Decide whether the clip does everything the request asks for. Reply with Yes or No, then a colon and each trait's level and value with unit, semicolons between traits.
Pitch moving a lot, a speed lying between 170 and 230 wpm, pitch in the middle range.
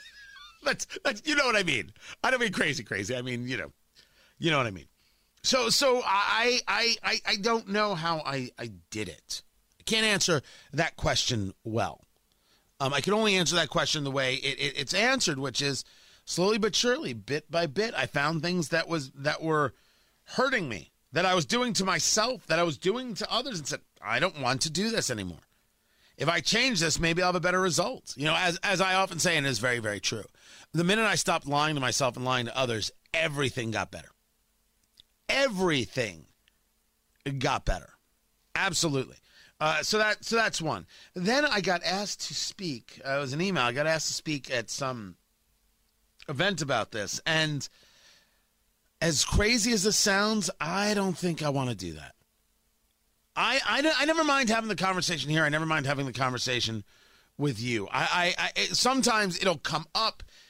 Yes: wide, 6.6 semitones; average, 195 wpm; medium, 165 Hz